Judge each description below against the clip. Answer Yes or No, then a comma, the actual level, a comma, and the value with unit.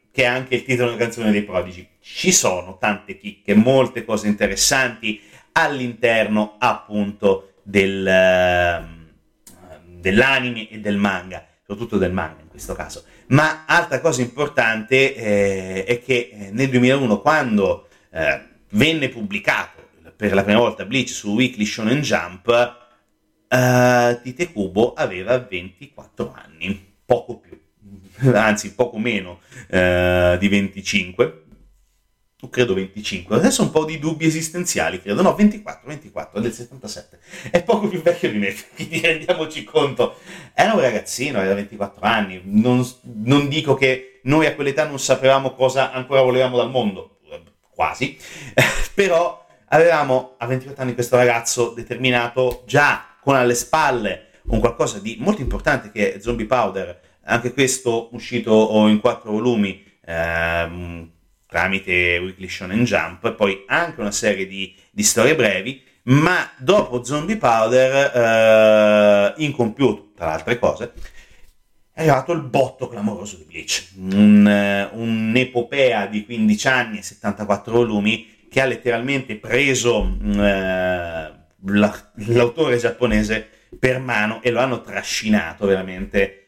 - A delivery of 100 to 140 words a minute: Yes, average, 130 wpm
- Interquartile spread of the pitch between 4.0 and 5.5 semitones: Yes, average, 4.5 semitones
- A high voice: No, low, 115 Hz